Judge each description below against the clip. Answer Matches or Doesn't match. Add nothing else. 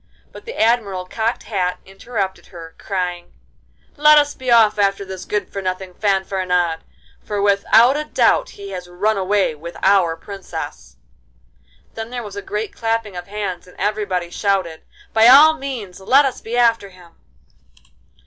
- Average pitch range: Matches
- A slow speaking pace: Doesn't match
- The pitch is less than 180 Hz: Doesn't match